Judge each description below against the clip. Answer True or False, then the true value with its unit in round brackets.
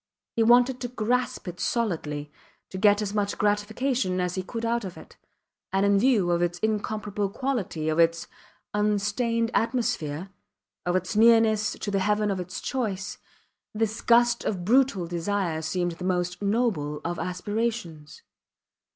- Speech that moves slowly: False (150 wpm)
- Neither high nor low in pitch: False (205 Hz)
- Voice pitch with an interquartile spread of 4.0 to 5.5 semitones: True (4.4 semitones)